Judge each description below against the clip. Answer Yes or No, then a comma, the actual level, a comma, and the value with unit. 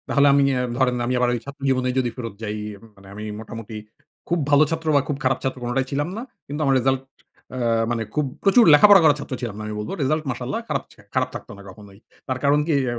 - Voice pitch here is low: Yes, low, 130 Hz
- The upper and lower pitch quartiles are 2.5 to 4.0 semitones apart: Yes, average, 3.3 semitones